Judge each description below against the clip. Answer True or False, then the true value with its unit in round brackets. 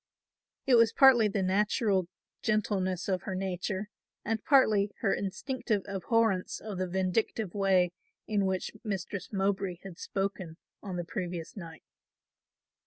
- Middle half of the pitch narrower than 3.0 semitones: True (2.4 semitones)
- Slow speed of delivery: True (130 wpm)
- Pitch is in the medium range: False (195 Hz)